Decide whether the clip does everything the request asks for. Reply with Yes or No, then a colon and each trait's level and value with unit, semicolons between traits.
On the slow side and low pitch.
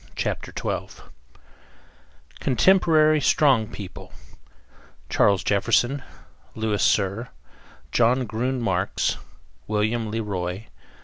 Yes: slow, 80 wpm; low, 110 Hz